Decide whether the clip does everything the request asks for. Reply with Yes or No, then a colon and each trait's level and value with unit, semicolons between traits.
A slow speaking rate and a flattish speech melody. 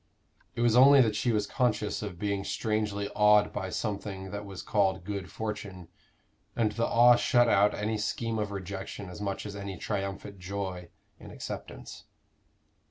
No: average, 165 wpm; narrow, 1.7 semitones